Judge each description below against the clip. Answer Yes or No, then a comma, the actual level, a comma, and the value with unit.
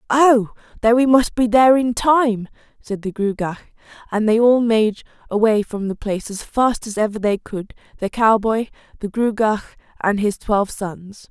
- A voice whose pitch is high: Yes, high, 220 Hz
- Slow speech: No, average, 175 wpm